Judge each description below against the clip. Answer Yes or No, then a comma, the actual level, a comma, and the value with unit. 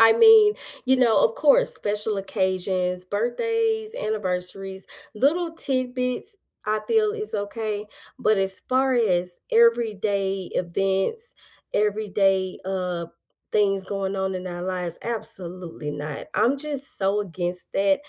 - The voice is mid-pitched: No, high, 205 Hz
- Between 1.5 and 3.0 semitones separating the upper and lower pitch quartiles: No, wide, 5.5 semitones